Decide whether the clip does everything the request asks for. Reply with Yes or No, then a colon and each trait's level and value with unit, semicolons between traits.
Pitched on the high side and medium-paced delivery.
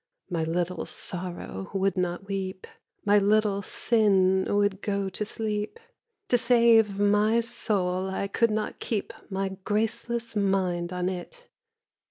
No: high, 200 Hz; slow, 130 wpm